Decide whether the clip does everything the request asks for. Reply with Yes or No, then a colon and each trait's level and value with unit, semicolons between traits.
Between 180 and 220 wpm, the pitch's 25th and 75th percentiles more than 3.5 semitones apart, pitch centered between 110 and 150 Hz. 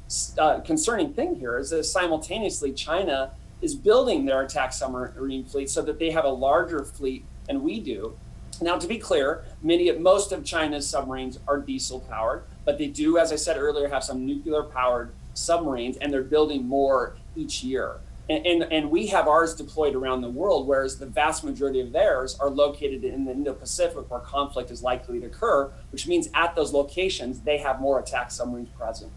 Yes: average, 185 wpm; average, 4.0 semitones; medium, 140 Hz